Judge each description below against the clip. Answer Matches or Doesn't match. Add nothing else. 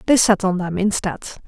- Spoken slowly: Doesn't match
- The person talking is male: Doesn't match